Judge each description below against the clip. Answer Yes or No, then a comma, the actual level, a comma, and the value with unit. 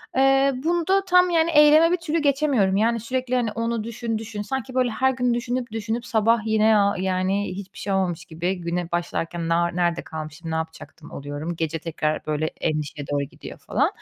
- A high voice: Yes, high, 215 Hz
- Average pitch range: No, wide, 7.0 semitones